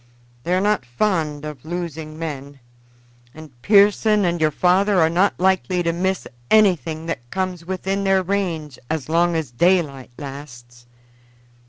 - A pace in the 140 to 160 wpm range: Yes, average, 145 wpm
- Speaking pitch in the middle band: Yes, medium, 170 Hz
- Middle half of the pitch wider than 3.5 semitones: Yes, average, 4.0 semitones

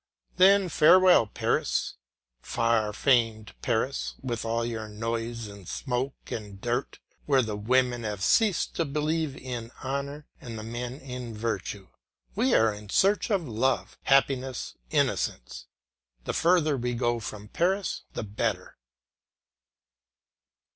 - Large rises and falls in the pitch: No, average, 4.1 semitones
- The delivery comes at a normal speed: No, slow, 125 wpm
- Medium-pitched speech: No, low, 120 Hz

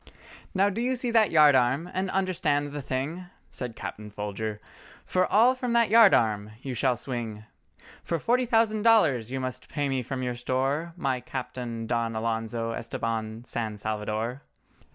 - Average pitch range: No, wide, 8.2 semitones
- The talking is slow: No, average, 160 wpm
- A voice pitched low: Yes, low, 130 Hz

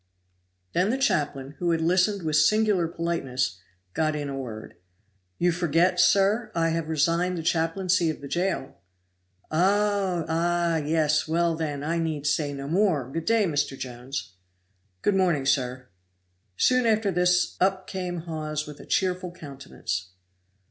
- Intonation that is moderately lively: Yes, average, 3.8 semitones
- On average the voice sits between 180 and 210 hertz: No, medium, 165 Hz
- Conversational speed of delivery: Yes, average, 150 wpm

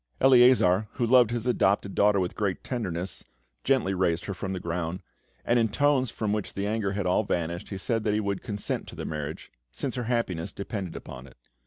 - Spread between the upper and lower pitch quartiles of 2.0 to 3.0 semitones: No, average, 4.4 semitones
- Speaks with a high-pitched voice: No, low, 100 Hz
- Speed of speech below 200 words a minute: No, fast, 205 wpm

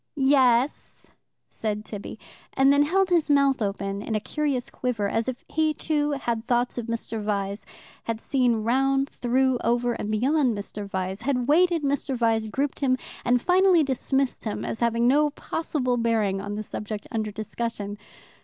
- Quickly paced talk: No, average, 170 wpm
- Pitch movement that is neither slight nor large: Yes, average, 4.3 semitones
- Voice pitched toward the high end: Yes, high, 245 Hz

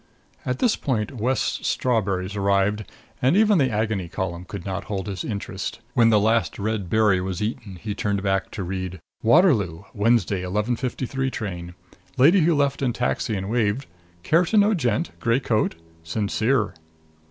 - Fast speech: No, average, 160 wpm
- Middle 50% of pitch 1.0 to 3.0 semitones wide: No, average, 4.7 semitones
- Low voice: Yes, low, 110 Hz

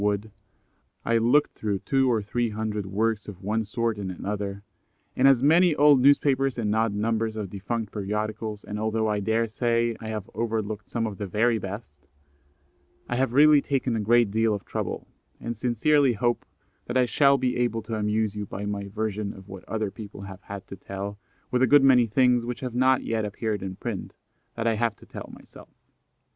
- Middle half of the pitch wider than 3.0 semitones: No, average, 2.7 semitones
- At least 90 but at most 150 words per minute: No, average, 195 wpm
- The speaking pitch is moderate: No, low, 110 Hz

